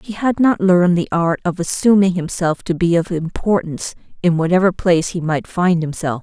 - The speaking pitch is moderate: Yes, medium, 175 Hz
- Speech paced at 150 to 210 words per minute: Yes, average, 195 wpm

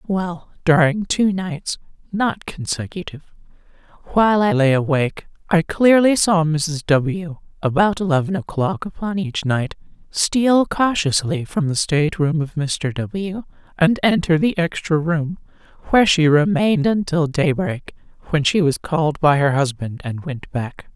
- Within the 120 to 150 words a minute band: Yes, average, 145 wpm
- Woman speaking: Yes, female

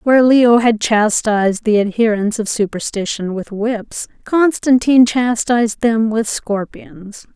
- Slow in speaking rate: Yes, slow, 120 wpm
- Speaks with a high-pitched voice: Yes, high, 225 Hz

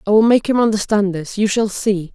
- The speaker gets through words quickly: Yes, fast, 250 wpm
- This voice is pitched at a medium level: No, high, 205 Hz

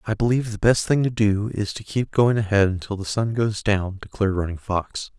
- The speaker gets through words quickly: Yes, fast, 230 wpm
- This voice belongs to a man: Yes, male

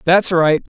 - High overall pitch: No, medium, 170 Hz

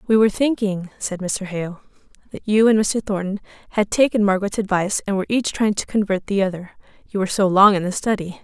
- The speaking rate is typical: No, fast, 215 wpm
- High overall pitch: Yes, high, 200 Hz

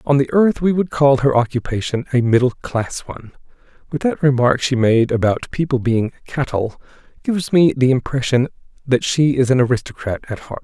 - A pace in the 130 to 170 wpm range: No, average, 180 wpm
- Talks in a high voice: No, low, 130 Hz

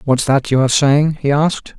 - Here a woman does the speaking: No, male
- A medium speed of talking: No, fast, 235 wpm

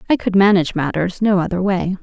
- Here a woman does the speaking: Yes, female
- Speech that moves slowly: No, fast, 205 wpm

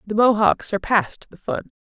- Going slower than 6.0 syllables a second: Yes, 5.0 syllables/s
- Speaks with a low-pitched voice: No, high, 205 Hz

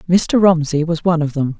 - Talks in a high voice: No, medium, 165 Hz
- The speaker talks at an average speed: No, fast, 225 wpm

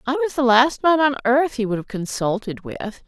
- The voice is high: Yes, very high, 250 Hz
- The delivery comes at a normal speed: No, fast, 235 wpm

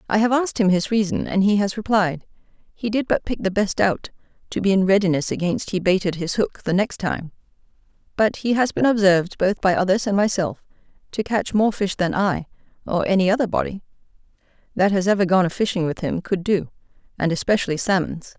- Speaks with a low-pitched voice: No, high, 195 Hz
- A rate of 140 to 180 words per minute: No, average, 200 wpm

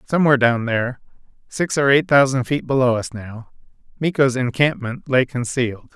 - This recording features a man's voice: Yes, male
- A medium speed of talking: No, slow, 130 wpm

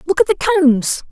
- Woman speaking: Yes, female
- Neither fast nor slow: No, fast, 215 wpm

